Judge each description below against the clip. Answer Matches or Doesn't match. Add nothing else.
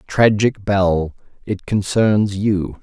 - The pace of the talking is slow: Matches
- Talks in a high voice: Doesn't match